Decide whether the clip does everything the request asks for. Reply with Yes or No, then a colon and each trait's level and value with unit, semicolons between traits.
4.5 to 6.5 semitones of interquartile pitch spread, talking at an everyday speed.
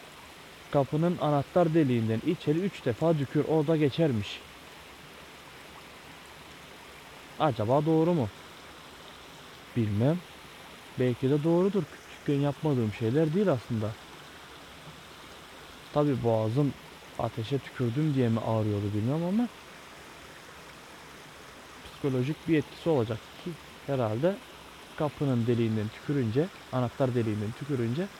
No: average, 5.2 semitones; slow, 90 wpm